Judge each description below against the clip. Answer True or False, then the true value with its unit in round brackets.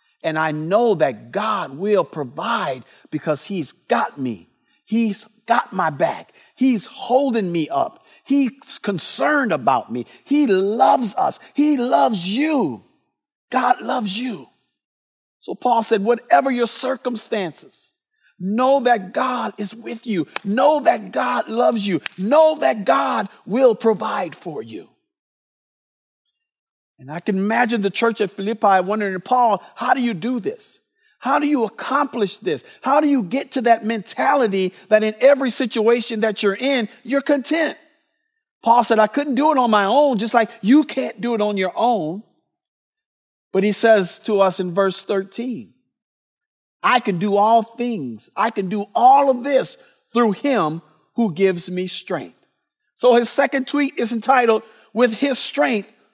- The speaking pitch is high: True (230 Hz)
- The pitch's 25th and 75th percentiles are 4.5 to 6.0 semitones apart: True (4.9 semitones)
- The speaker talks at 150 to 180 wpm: True (155 wpm)